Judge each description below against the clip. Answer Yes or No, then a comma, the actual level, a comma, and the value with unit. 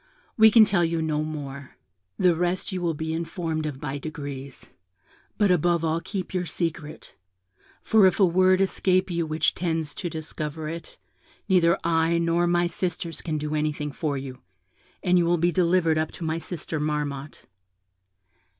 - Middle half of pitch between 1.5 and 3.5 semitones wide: Yes, narrow, 2.5 semitones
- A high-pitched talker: No, medium, 165 Hz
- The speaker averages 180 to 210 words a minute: No, average, 170 wpm